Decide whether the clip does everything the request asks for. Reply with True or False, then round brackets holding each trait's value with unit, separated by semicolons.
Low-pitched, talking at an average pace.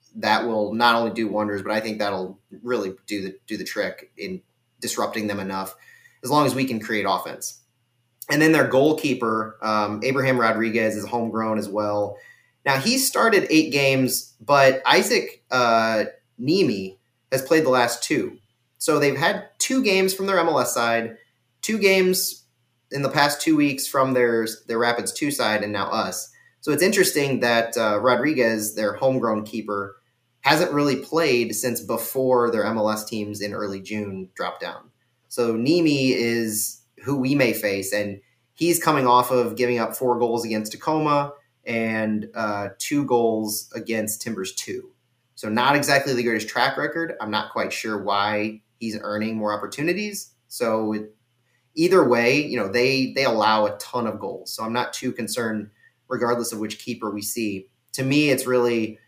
True (120 Hz; 170 wpm)